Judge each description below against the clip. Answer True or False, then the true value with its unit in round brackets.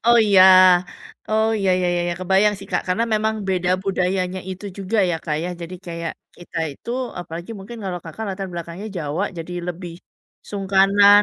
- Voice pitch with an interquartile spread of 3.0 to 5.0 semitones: False (2.5 semitones)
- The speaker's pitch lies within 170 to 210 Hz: True (190 Hz)